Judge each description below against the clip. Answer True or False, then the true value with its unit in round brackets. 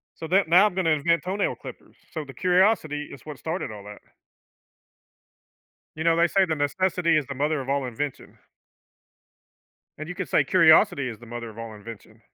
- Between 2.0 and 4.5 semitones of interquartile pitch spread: False (5.5 semitones)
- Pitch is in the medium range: True (155 Hz)